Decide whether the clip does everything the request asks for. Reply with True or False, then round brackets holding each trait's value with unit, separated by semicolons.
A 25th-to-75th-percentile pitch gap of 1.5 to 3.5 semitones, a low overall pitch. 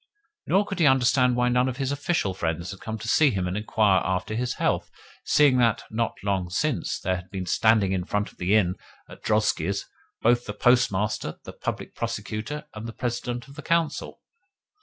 False (4.7 semitones; 110 Hz)